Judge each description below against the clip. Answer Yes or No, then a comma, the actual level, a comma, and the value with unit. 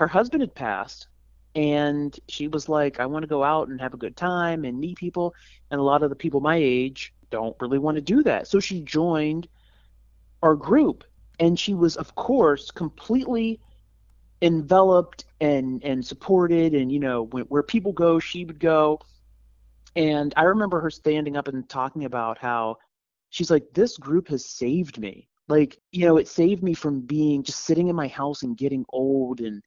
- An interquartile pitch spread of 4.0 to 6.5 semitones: Yes, average, 4.4 semitones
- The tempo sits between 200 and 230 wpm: No, average, 190 wpm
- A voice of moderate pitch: Yes, medium, 150 Hz